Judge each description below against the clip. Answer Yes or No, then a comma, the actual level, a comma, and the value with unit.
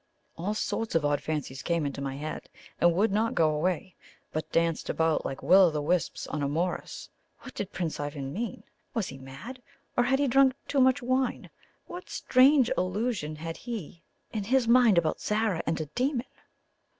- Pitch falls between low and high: Yes, medium, 180 Hz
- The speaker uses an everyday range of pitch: No, wide, 7.6 semitones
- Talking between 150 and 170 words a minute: No, average, 185 wpm